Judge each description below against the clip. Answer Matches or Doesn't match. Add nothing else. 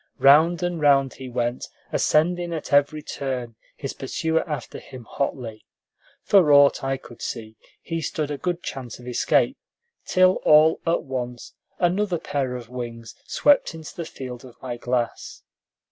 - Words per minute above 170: Doesn't match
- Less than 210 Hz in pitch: Matches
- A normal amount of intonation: Matches